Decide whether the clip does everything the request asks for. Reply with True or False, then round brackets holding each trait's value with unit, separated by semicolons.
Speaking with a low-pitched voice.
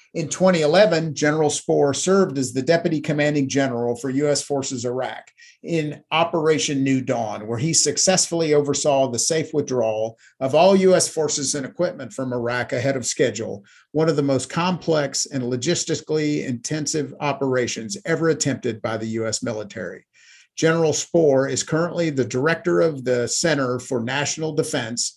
False (145 Hz)